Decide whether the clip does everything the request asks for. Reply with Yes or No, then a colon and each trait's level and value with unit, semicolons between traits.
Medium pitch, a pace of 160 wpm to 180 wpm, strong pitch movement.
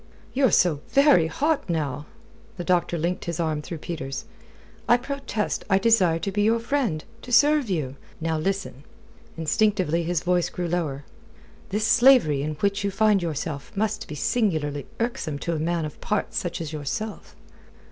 Yes: medium, 175 Hz; average, 165 wpm; wide, 5.7 semitones